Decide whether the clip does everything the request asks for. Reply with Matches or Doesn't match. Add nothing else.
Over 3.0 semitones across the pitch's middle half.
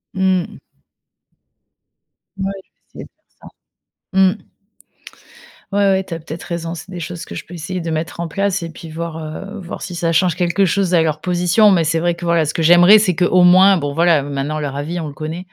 Doesn't match